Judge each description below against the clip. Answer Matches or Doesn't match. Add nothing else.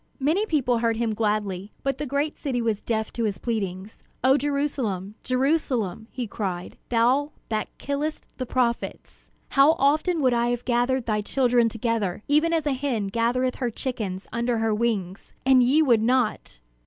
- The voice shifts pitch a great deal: Doesn't match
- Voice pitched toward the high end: Matches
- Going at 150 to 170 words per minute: Matches